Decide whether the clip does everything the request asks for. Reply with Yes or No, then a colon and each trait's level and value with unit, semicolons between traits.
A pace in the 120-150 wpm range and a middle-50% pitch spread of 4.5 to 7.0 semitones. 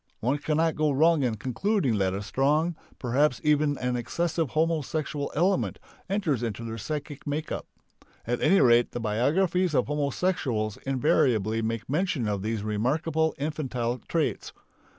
Yes: average, 145 wpm; average, 5.2 semitones